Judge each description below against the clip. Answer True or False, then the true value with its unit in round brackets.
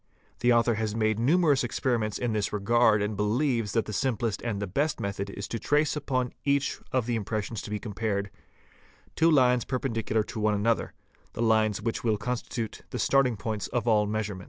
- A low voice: True (115 Hz)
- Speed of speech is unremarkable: True (185 wpm)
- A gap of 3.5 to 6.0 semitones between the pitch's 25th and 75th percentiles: False (2.9 semitones)